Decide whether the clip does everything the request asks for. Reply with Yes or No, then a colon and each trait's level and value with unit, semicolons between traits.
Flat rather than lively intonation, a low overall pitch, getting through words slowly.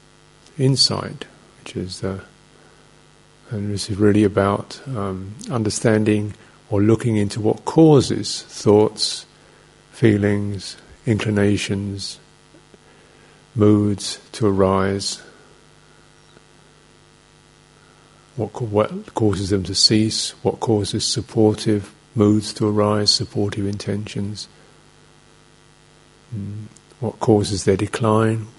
Yes: narrow, 1.6 semitones; low, 105 Hz; slow, 90 wpm